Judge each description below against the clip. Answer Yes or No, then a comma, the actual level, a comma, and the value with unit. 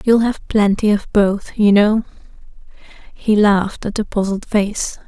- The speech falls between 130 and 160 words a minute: Yes, average, 155 wpm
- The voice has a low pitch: No, high, 210 Hz